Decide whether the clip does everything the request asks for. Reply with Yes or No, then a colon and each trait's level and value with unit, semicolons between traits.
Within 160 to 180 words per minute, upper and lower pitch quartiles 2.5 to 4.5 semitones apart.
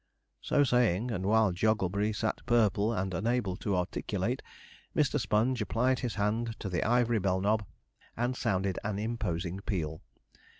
No: average, 145 wpm; average, 3.5 semitones